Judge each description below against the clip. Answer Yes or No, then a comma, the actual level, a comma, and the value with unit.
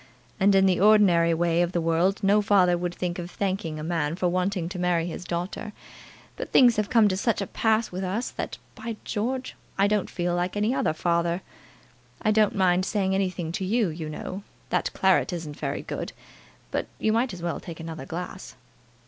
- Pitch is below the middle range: No, medium, 185 Hz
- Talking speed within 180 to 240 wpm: Yes, average, 200 wpm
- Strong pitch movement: No, average, 3.1 semitones